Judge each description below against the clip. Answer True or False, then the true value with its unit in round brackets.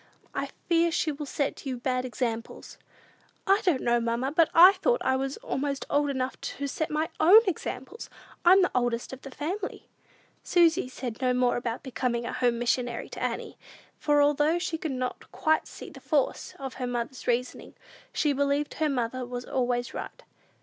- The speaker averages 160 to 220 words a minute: True (180 wpm)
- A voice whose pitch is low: False (270 Hz)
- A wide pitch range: False (4.0 semitones)